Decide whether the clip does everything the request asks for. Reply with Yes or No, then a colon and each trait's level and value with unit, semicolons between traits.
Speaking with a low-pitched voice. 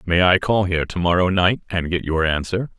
Yes: very low, 90 Hz